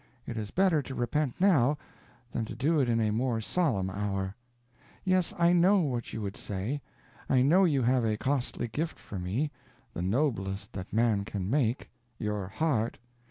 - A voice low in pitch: Yes, low, 120 Hz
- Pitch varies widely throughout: Yes, wide, 6.2 semitones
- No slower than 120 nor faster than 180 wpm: Yes, average, 175 wpm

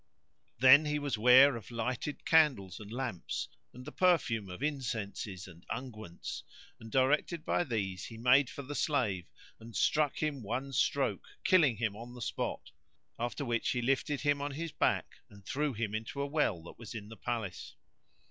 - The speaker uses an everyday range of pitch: Yes, average, 4.7 semitones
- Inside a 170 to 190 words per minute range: Yes, average, 175 wpm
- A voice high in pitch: No, low, 125 Hz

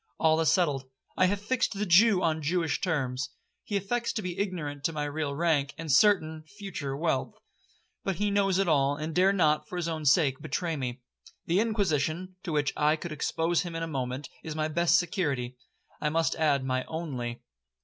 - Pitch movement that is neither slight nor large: Yes, average, 4.1 semitones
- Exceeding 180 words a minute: Yes, average, 190 wpm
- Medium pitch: Yes, medium, 160 Hz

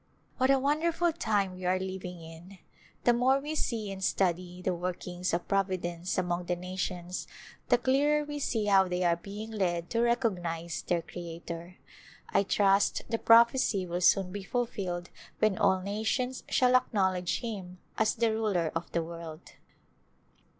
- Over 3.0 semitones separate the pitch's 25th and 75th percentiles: Yes, average, 4.5 semitones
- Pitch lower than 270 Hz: Yes, high, 190 Hz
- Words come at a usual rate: Yes, average, 160 wpm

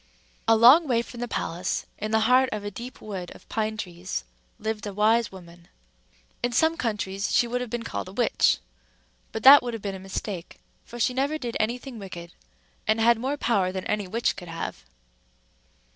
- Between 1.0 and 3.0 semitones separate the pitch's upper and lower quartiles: No, average, 3.9 semitones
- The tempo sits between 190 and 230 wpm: Yes, average, 200 wpm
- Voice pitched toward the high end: Yes, high, 220 Hz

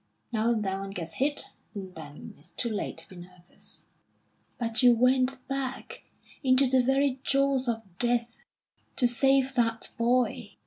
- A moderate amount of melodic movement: Yes, average, 3.3 semitones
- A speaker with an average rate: Yes, average, 155 wpm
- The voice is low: No, high, 245 Hz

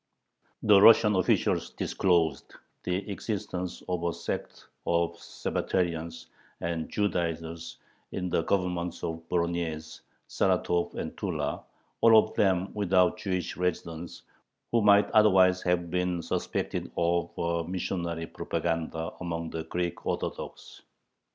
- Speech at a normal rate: No, slow, 115 wpm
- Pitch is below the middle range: Yes, very low, 85 Hz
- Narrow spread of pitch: Yes, narrow, 1.8 semitones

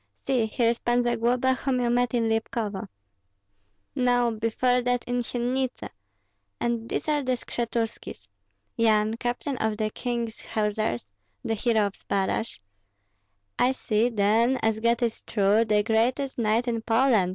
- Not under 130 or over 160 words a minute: Yes, average, 150 wpm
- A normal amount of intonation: No, narrow, 2.2 semitones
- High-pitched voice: Yes, high, 230 Hz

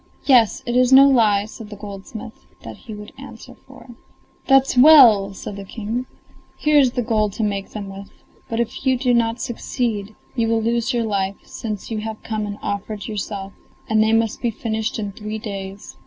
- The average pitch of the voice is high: Yes, high, 220 Hz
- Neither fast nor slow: Yes, average, 195 wpm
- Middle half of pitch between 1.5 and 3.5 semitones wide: Yes, narrow, 2.6 semitones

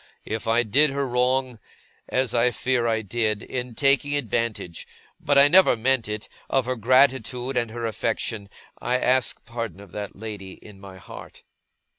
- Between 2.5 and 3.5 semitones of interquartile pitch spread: Yes, average, 3.0 semitones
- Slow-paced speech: No, average, 165 wpm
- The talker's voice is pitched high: No, low, 120 Hz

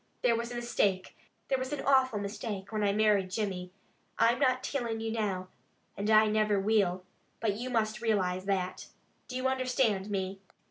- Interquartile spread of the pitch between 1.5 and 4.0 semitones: Yes, average, 3.3 semitones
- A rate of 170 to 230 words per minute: Yes, average, 175 wpm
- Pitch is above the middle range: Yes, high, 215 Hz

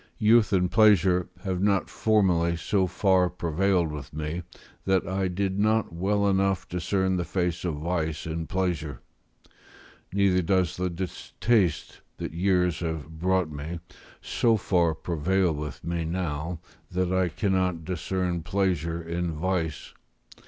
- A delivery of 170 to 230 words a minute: No, slow, 135 wpm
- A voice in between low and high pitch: No, very low, 90 Hz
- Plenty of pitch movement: No, narrow, 2.4 semitones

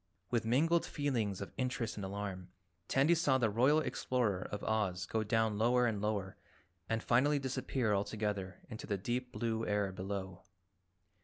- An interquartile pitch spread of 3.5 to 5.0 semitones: Yes, average, 3.8 semitones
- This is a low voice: Yes, low, 110 Hz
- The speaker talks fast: No, average, 155 wpm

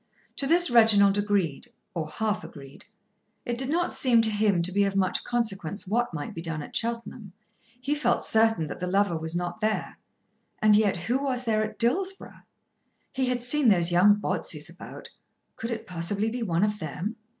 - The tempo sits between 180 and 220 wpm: Yes, average, 185 wpm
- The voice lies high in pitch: Yes, high, 210 Hz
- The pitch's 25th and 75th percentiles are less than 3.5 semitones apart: No, average, 4.8 semitones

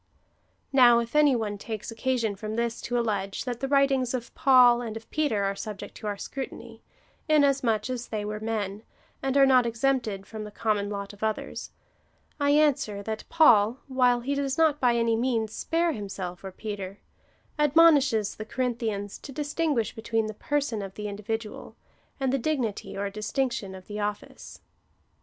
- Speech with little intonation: No, average, 4.2 semitones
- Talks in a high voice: Yes, high, 230 Hz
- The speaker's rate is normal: Yes, average, 170 wpm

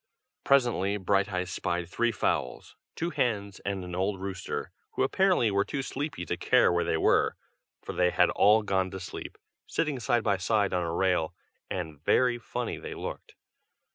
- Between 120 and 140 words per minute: No, average, 170 wpm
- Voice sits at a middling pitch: No, low, 100 Hz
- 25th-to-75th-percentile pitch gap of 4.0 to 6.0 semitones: Yes, average, 4.7 semitones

